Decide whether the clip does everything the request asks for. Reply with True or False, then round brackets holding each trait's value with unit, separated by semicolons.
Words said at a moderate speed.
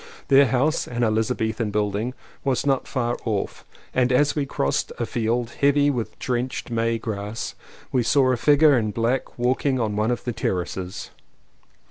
True (165 wpm)